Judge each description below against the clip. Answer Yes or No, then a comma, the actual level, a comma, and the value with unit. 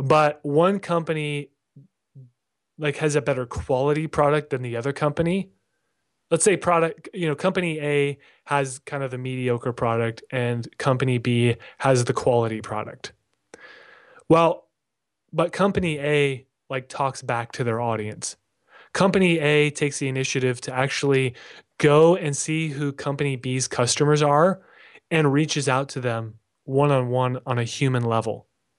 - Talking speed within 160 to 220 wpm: No, average, 140 wpm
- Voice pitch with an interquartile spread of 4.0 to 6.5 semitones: No, average, 3.2 semitones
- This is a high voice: No, medium, 140 Hz